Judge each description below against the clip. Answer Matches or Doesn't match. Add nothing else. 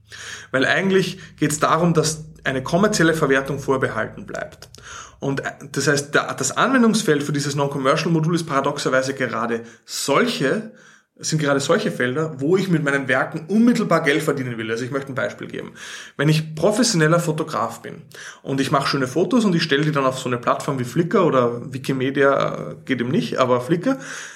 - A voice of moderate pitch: Matches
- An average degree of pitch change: Matches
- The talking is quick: Doesn't match